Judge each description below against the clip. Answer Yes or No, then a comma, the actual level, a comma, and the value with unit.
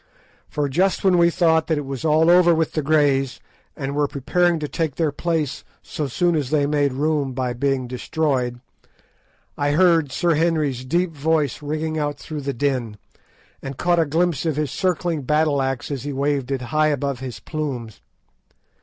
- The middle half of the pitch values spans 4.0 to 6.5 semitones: No, average, 3.0 semitones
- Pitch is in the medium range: Yes, medium, 150 Hz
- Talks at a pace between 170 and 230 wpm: Yes, average, 180 wpm